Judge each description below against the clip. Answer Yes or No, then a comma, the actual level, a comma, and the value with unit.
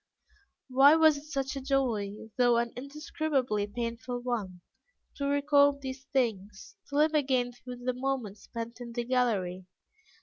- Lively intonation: No, average, 3.2 semitones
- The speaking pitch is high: Yes, very high, 250 Hz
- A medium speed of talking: Yes, average, 145 wpm